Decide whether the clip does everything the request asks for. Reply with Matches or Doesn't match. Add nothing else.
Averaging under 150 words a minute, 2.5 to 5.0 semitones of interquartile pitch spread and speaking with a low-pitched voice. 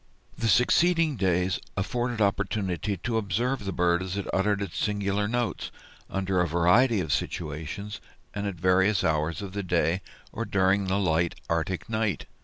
Doesn't match